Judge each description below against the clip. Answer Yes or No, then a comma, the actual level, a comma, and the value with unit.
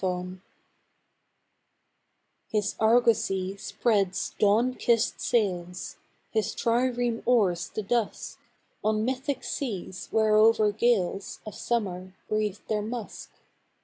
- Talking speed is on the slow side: Yes, slow, 95 wpm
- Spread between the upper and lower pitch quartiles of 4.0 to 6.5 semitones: No, average, 3.5 semitones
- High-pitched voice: Yes, high, 215 Hz